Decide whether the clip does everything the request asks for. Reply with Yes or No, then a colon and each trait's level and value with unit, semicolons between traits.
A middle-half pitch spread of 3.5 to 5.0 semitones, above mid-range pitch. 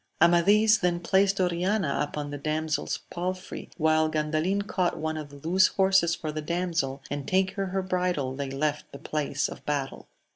No: average, 3.8 semitones; medium, 170 Hz